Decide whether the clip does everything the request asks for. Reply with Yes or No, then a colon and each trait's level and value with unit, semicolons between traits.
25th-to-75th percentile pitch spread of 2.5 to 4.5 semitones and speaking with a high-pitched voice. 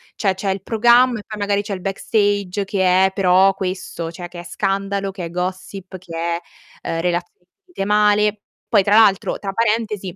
No: narrow, 2.1 semitones; high, 195 Hz